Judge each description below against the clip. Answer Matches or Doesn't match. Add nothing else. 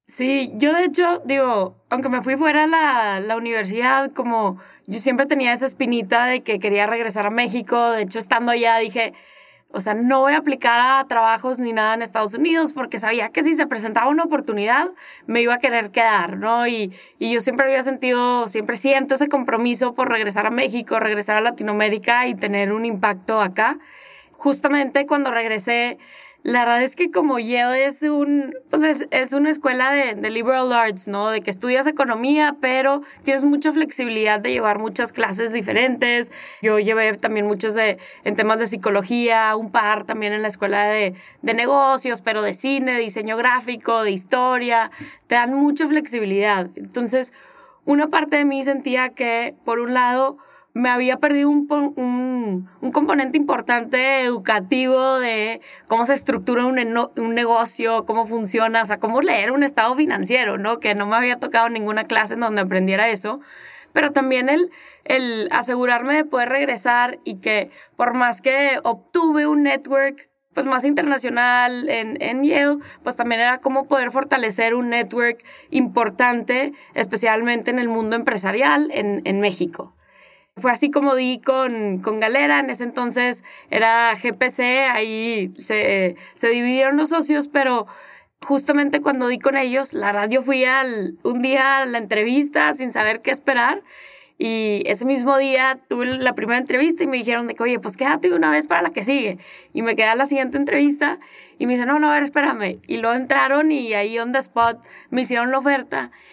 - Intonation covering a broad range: Doesn't match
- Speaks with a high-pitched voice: Matches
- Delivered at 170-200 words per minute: Matches